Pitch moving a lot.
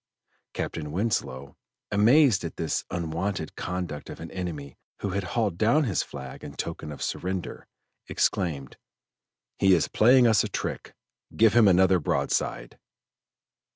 No: average, 4.7 semitones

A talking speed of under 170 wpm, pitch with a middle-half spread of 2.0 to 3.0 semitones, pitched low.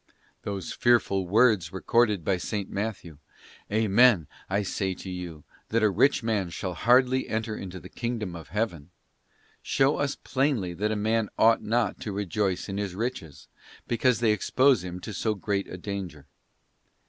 No: average, 160 wpm; average, 3.7 semitones; low, 105 Hz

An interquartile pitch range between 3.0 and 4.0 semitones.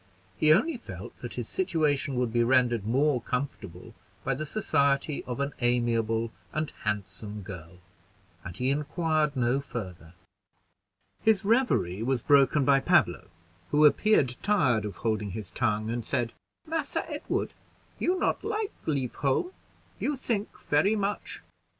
No: wide, 5.4 semitones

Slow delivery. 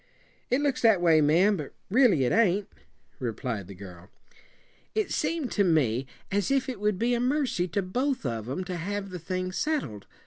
No: average, 185 wpm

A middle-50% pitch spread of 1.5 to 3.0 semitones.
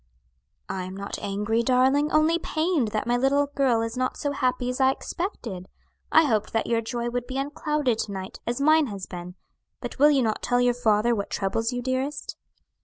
No: average, 4.2 semitones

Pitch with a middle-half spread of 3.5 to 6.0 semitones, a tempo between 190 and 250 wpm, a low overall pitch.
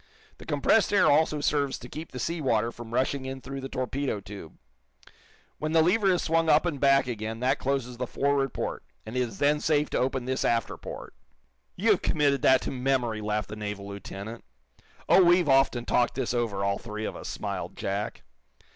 Yes: average, 4.3 semitones; average, 200 wpm; low, 130 Hz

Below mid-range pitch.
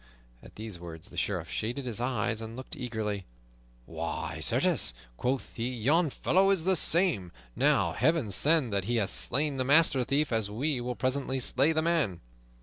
Yes: low, 125 Hz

